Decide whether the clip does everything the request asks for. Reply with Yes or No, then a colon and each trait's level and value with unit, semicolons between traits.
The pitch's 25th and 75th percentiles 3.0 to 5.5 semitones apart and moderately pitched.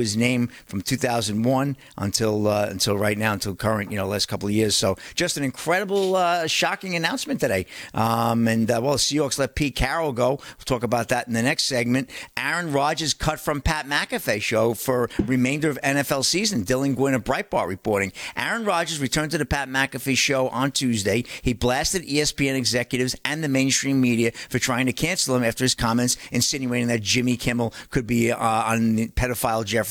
No: average, 3.7 semitones; low, 125 Hz